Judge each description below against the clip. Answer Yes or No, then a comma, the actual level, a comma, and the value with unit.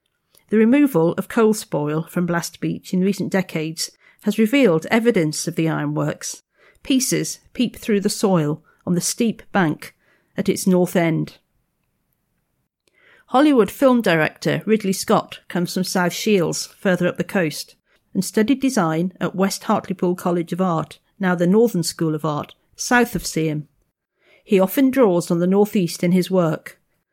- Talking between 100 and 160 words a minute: Yes, average, 155 wpm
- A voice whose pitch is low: No, medium, 185 Hz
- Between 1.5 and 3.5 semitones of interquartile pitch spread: No, average, 4.3 semitones